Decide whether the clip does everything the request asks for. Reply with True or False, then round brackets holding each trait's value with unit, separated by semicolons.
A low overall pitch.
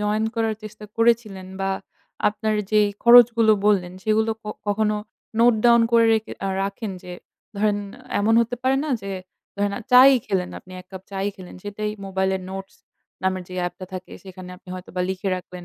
False (205 Hz)